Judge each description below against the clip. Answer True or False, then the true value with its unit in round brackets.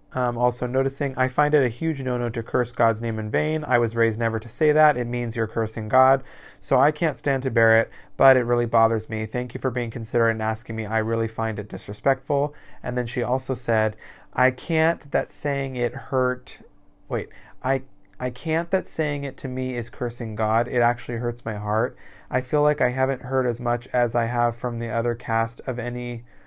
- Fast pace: True (220 wpm)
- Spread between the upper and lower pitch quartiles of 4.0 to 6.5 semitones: False (2.5 semitones)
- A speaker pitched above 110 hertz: True (125 Hz)